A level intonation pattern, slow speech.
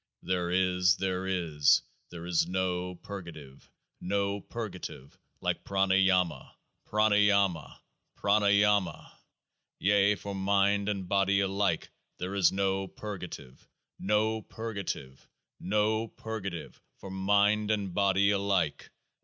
Yes: narrow, 2.0 semitones; slow, 120 wpm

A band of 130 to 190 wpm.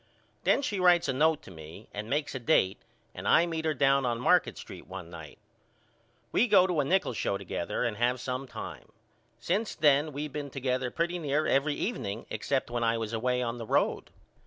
No: fast, 205 wpm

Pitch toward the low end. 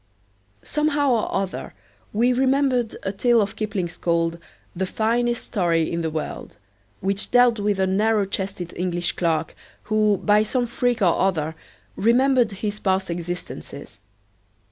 No: high, 205 Hz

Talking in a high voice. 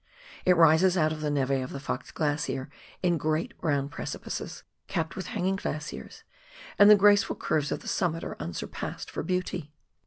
No: medium, 160 Hz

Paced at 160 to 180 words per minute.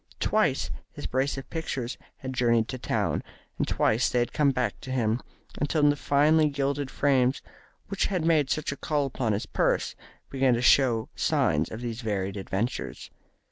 Yes: average, 175 wpm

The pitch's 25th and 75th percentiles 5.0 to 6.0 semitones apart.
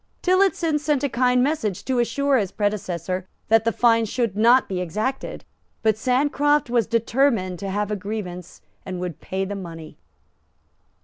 Yes: wide, 5.5 semitones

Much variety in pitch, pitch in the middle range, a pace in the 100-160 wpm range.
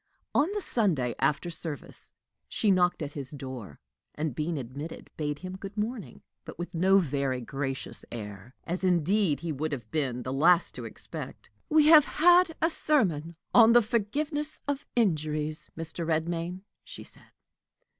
Yes: wide, 6.5 semitones; medium, 165 Hz; average, 155 wpm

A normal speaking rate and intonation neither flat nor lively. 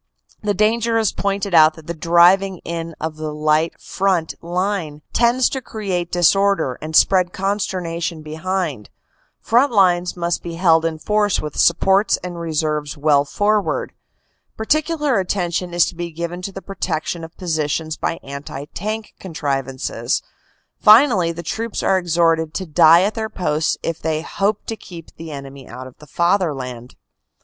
Yes: average, 155 wpm; average, 3.9 semitones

